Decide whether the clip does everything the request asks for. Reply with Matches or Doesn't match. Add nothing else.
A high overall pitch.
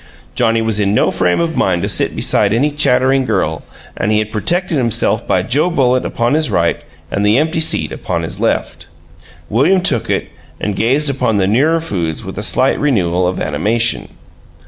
Doesn't match